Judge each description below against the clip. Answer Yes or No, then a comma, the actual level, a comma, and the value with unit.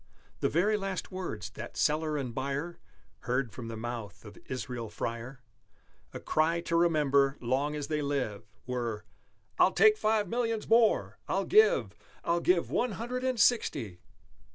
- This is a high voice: No, medium, 145 Hz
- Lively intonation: Yes, wide, 7.9 semitones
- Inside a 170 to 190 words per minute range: No, average, 155 wpm